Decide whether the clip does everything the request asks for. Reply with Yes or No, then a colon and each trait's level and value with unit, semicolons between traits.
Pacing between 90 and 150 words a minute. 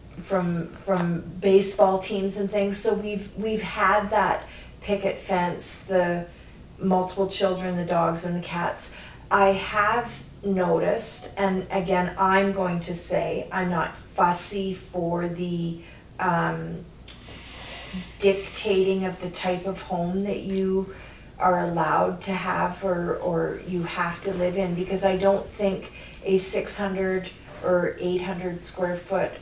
Yes: slow, 135 wpm